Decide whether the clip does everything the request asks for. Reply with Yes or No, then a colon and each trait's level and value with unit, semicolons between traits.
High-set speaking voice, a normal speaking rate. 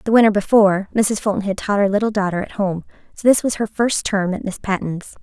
No: high, 200 Hz; fast, 240 wpm